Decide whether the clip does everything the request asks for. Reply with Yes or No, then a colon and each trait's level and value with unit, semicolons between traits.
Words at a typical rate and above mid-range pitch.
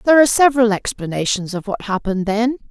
Yes: average, 180 wpm; high, 220 Hz